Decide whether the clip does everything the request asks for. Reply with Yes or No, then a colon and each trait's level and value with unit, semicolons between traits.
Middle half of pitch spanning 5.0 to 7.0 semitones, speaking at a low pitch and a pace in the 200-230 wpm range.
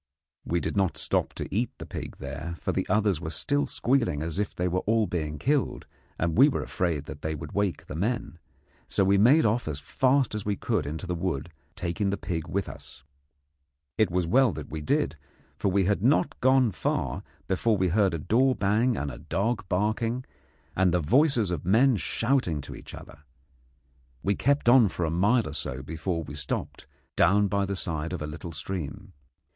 Yes: wide, 5.6 semitones; very low, 95 Hz; fast, 205 wpm